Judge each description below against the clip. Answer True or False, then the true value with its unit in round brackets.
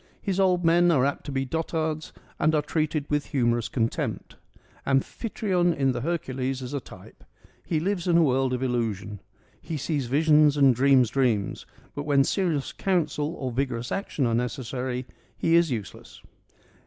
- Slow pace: False (165 wpm)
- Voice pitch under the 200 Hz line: True (140 Hz)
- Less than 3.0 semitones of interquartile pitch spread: False (4.3 semitones)